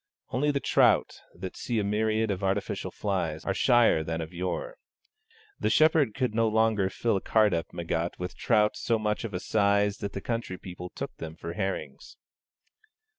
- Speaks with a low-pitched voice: Yes, low, 100 Hz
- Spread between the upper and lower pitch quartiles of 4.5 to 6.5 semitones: No, average, 3.6 semitones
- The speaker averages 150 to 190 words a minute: Yes, average, 180 wpm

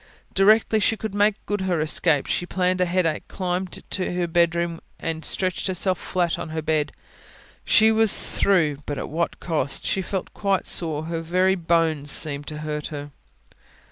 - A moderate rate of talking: Yes, average, 175 wpm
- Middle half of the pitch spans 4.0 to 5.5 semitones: No, average, 3.1 semitones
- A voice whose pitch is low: No, medium, 175 Hz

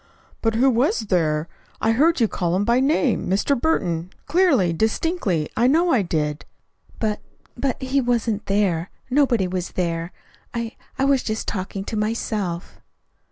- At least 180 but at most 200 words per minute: No, average, 155 wpm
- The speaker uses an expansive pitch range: Yes, wide, 6.4 semitones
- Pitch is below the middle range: No, high, 220 Hz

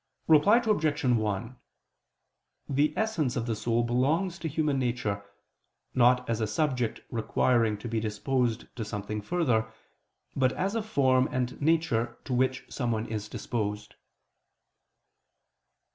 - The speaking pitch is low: Yes, low, 125 Hz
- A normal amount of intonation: Yes, average, 4.9 semitones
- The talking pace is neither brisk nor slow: No, slow, 130 wpm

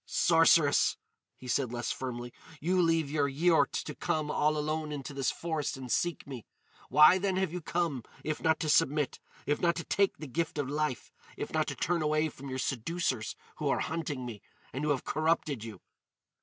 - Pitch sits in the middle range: Yes, medium, 150 Hz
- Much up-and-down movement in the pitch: No, average, 3.6 semitones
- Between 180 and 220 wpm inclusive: Yes, average, 185 wpm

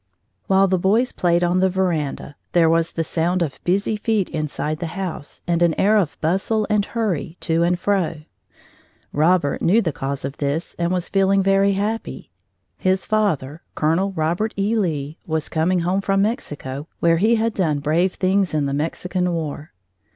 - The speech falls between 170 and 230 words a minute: Yes, average, 175 wpm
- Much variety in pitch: No, average, 3.7 semitones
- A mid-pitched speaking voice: Yes, medium, 175 Hz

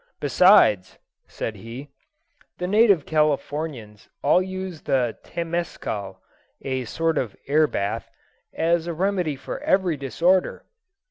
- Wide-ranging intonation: Yes, wide, 5.7 semitones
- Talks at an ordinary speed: No, slow, 115 wpm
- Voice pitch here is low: No, medium, 155 Hz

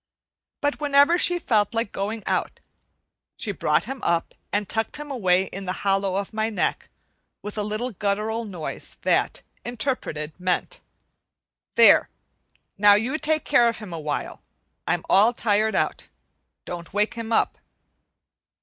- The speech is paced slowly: No, average, 145 wpm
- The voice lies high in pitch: Yes, high, 215 Hz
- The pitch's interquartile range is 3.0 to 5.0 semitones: Yes, average, 3.5 semitones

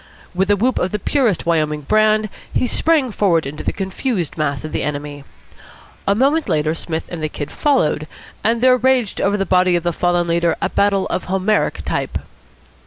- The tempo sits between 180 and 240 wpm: Yes, average, 190 wpm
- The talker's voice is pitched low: No, medium, 185 Hz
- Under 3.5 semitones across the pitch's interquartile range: No, average, 5.2 semitones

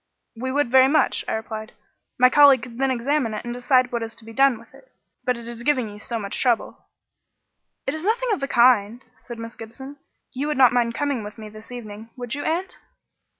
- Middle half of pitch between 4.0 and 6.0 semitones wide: No, average, 3.1 semitones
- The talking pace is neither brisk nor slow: No, fast, 225 wpm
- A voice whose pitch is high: Yes, high, 245 Hz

